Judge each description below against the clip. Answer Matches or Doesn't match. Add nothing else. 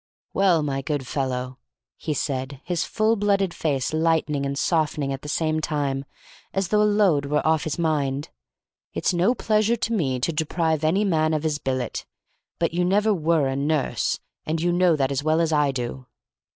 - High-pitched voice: Doesn't match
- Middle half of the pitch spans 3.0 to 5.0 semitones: Matches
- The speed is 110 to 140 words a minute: Doesn't match